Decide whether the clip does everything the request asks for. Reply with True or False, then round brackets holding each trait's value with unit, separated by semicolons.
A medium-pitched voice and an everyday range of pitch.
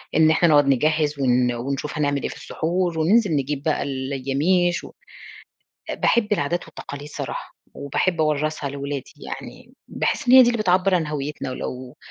True (150 Hz; 4.0 semitones)